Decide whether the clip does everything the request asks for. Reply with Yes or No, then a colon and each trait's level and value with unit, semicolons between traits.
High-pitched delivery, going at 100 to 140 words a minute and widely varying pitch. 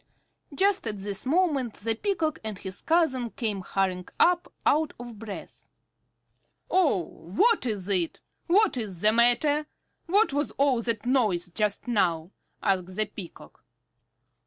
Yes: high, 230 Hz; slow, 135 wpm; wide, 7.4 semitones